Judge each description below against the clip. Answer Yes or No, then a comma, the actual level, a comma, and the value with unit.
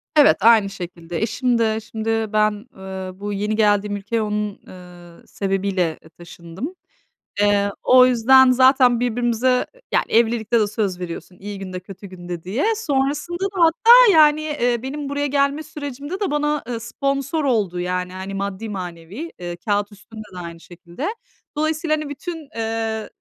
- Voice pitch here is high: Yes, high, 220 Hz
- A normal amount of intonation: No, wide, 6.4 semitones